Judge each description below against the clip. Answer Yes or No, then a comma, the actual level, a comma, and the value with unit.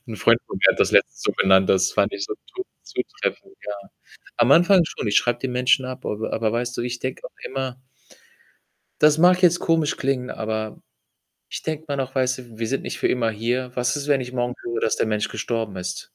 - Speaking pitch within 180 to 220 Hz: No, low, 125 Hz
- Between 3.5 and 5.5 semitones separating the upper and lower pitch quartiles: Yes, average, 3.9 semitones